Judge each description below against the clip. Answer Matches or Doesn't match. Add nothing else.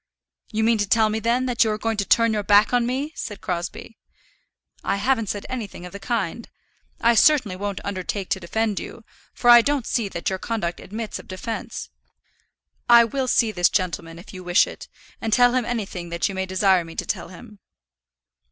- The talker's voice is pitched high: Matches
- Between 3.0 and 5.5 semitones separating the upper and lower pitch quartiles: Matches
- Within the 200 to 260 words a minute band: Matches